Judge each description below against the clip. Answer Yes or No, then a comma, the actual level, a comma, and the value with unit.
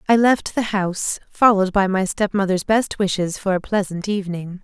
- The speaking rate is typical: Yes, average, 180 wpm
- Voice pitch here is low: No, high, 195 Hz